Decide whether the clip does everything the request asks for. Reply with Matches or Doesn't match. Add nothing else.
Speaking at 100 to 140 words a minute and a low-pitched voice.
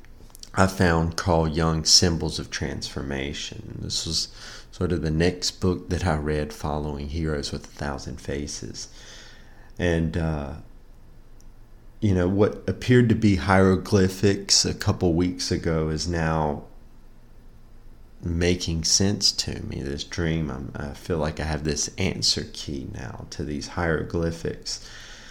Matches